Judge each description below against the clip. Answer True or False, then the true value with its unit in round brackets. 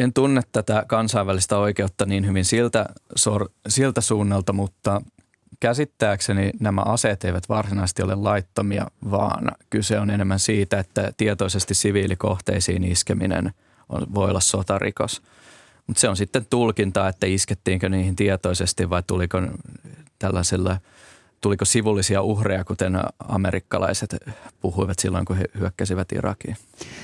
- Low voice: True (100 Hz)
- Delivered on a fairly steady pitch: True (2.3 semitones)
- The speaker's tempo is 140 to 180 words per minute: False (120 wpm)